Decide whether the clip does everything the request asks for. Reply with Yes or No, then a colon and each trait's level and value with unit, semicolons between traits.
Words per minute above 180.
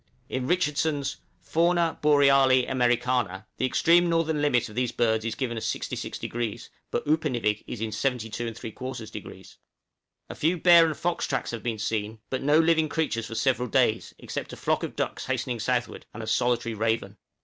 No: average, 175 wpm